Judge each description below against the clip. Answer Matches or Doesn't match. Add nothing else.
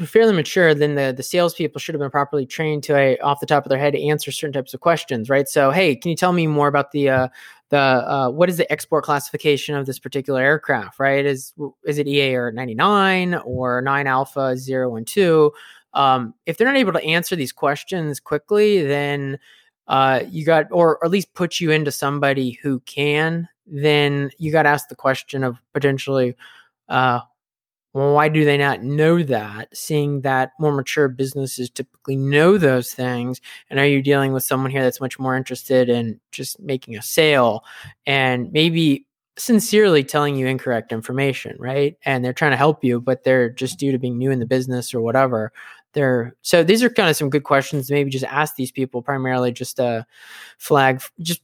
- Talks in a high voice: Doesn't match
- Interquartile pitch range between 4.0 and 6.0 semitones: Doesn't match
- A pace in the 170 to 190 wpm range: Doesn't match